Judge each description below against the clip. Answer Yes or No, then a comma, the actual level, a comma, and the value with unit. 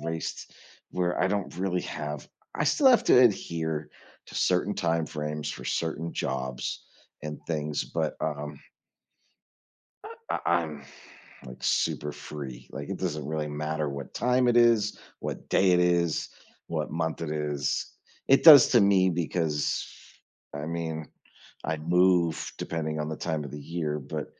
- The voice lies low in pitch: Yes, very low, 80 Hz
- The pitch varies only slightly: No, average, 3.0 semitones